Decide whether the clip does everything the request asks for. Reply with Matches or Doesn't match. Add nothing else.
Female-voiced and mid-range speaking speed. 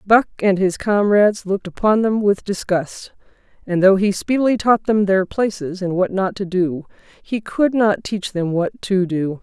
Matches